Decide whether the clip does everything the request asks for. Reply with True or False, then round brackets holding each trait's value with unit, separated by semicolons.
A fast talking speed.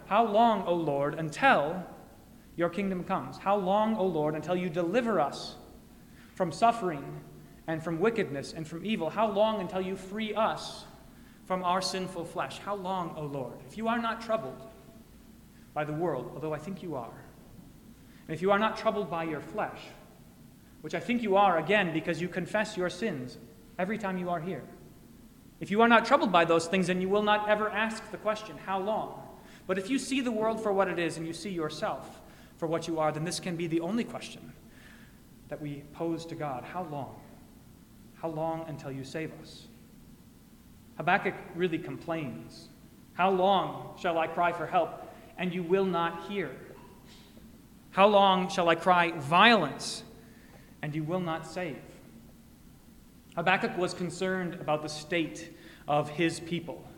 False (175 wpm)